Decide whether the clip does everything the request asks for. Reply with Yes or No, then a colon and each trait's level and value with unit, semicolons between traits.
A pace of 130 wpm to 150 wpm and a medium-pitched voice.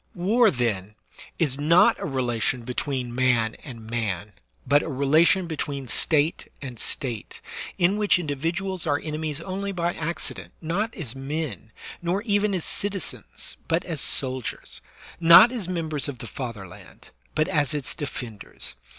Yes: average, 145 wpm; medium, 150 Hz